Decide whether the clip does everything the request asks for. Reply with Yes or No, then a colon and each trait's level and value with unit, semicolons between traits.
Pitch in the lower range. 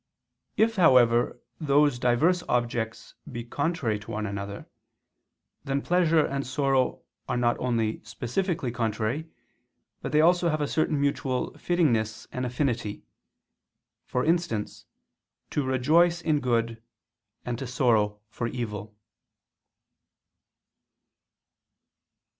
Yes: low, 125 Hz